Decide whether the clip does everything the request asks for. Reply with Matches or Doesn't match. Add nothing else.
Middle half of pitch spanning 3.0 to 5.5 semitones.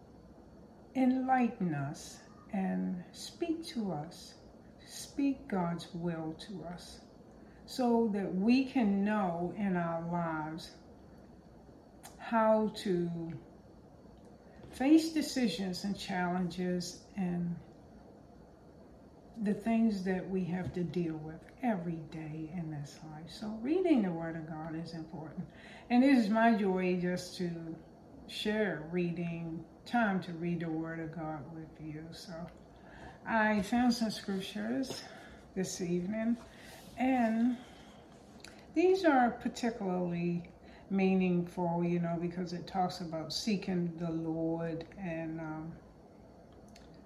Matches